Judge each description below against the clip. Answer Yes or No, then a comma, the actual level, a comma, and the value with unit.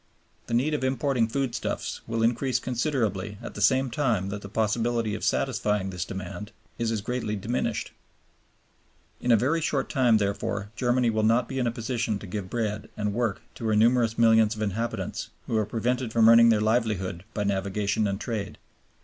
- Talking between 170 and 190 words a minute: Yes, average, 185 wpm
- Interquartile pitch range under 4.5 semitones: Yes, average, 2.7 semitones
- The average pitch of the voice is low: Yes, low, 115 Hz